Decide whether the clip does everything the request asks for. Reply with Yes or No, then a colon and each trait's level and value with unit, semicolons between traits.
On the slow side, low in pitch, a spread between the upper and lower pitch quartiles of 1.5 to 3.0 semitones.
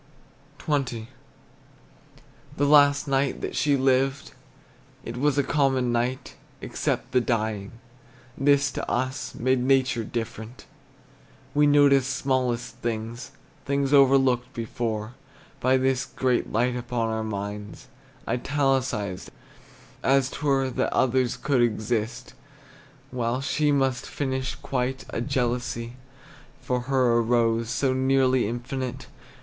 Yes: slow, 115 wpm; low, 130 Hz; narrow, 2.4 semitones